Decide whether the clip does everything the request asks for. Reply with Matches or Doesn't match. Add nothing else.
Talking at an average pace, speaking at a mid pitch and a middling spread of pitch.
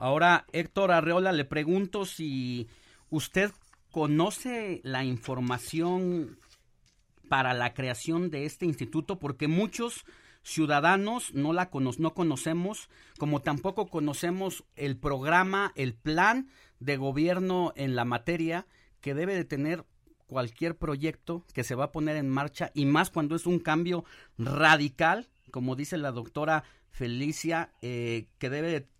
Matches